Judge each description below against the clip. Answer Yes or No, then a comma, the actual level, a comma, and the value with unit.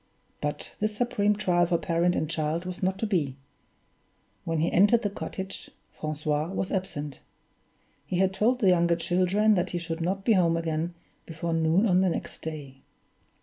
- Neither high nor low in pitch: Yes, medium, 175 Hz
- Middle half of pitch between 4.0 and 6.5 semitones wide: No, average, 3.0 semitones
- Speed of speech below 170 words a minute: No, average, 175 wpm